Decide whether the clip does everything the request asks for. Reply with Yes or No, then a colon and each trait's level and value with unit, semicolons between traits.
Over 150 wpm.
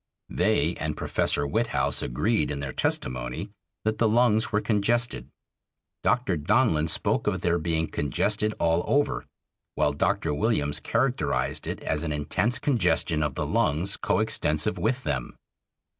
No: average, 140 wpm